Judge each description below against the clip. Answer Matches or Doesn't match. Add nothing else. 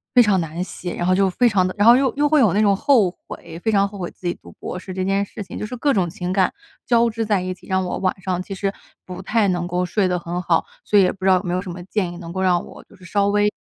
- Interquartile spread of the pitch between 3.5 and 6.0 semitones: Doesn't match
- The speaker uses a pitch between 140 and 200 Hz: Matches